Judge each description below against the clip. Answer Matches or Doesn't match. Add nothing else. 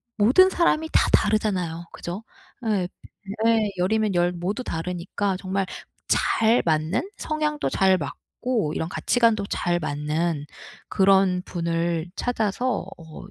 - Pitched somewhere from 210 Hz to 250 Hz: Doesn't match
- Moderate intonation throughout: Matches